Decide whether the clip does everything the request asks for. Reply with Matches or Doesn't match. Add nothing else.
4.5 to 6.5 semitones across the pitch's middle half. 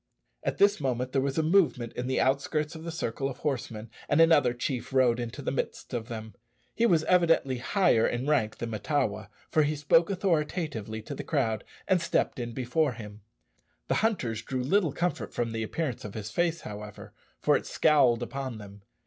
Matches